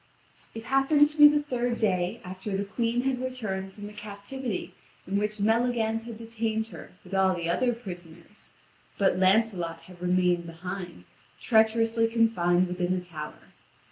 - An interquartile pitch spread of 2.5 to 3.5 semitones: No, average, 4.1 semitones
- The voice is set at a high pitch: Yes, high, 210 Hz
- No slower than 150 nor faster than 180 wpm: Yes, average, 155 wpm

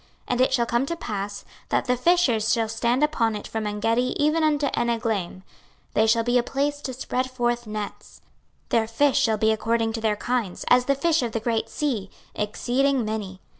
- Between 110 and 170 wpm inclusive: No, average, 200 wpm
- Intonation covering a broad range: No, average, 3.0 semitones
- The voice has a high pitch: Yes, high, 235 Hz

